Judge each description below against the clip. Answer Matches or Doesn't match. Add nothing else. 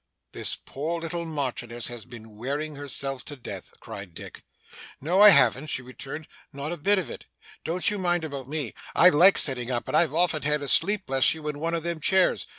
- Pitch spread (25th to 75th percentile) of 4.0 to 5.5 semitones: Matches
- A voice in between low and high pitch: Matches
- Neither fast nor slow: Doesn't match